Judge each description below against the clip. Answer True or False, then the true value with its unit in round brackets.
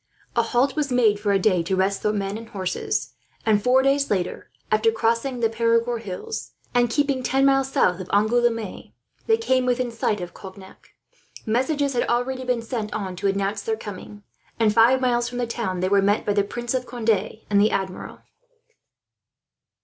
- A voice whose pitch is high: True (225 Hz)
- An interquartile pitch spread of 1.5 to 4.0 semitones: True (3.6 semitones)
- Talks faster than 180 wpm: True (190 wpm)